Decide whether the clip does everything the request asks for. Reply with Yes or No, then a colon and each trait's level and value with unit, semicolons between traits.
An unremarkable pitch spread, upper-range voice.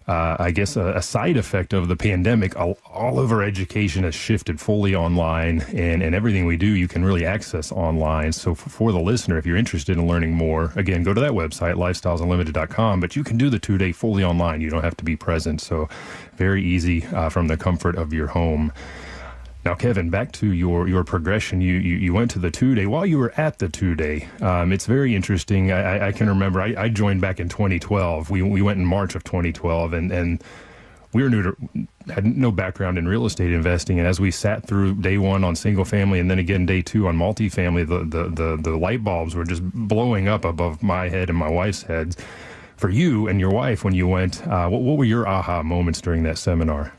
No: average, 3.1 semitones; very low, 90 Hz